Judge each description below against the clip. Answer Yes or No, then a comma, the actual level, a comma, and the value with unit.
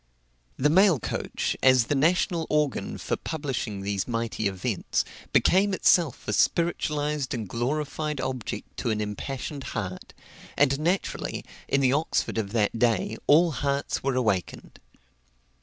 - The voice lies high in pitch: No, low, 135 Hz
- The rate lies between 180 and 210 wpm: No, slow, 135 wpm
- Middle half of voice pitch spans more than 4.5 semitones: Yes, average, 5.1 semitones